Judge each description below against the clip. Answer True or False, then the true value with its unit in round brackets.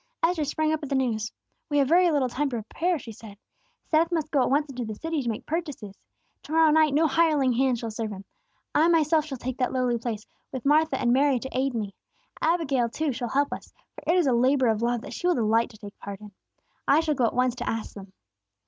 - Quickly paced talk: True (245 wpm)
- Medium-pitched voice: False (265 Hz)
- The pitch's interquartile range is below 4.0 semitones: False (4.9 semitones)